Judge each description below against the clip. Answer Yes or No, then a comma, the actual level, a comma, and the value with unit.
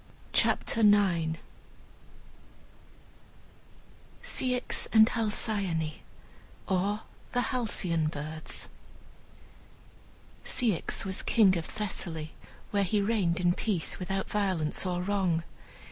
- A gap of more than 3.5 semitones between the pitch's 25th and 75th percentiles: Yes, average, 4.0 semitones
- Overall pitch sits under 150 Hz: No, high, 190 Hz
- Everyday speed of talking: No, slow, 85 wpm